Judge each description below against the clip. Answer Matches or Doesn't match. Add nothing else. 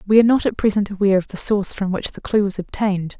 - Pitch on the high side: Matches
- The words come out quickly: Matches